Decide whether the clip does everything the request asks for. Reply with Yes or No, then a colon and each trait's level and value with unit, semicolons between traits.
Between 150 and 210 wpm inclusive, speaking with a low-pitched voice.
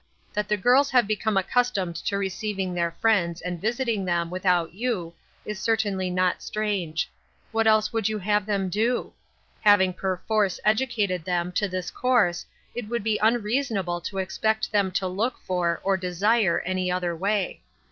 No: average, 165 wpm; high, 200 Hz